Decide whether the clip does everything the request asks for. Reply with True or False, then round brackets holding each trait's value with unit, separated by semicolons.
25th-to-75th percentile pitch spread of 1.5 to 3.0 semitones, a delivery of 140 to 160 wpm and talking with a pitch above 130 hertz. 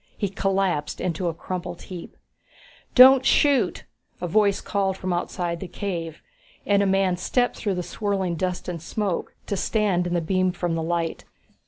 False (2.5 semitones; 170 wpm; 185 Hz)